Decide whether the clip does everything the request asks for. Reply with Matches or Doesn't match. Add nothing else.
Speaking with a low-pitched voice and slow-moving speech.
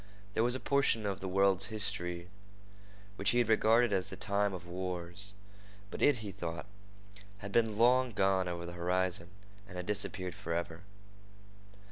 Doesn't match